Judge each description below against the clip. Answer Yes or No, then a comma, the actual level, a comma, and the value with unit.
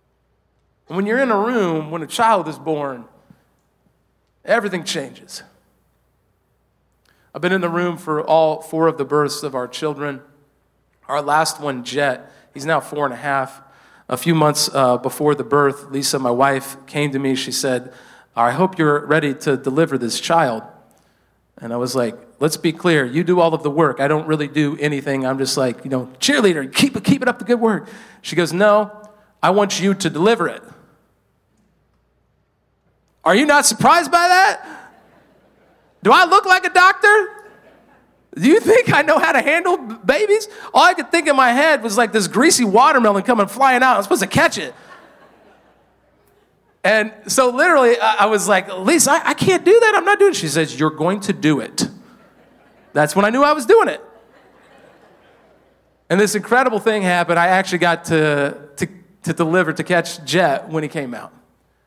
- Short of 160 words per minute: No, average, 185 wpm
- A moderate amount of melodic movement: No, wide, 8.3 semitones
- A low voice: No, medium, 170 Hz